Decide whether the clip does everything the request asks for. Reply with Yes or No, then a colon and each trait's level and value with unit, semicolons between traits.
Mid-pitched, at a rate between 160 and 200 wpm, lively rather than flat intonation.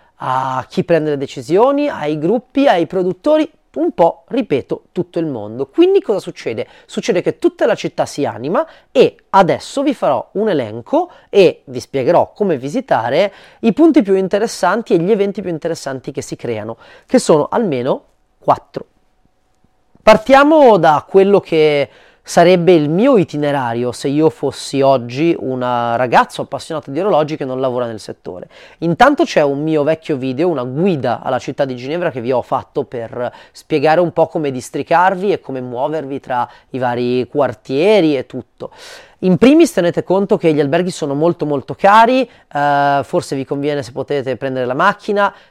Yes: medium, 165 Hz; average, 165 wpm; wide, 7.0 semitones